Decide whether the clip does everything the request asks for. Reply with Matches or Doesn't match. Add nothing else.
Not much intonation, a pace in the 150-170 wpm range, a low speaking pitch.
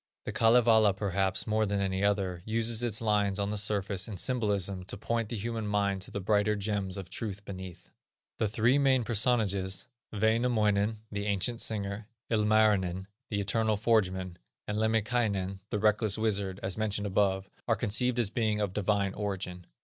Matches